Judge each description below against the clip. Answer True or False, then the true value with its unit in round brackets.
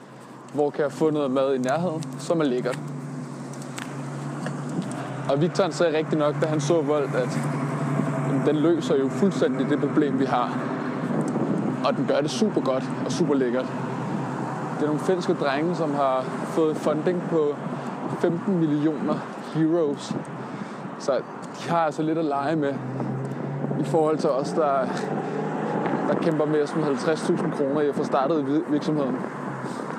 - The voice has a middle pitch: True (150 Hz)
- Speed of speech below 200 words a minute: True (150 wpm)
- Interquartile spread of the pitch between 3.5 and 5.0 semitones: False (3.1 semitones)